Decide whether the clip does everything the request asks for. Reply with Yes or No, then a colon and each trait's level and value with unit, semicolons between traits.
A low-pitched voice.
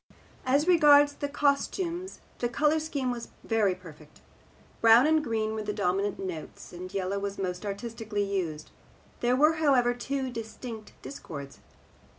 No: high, 230 Hz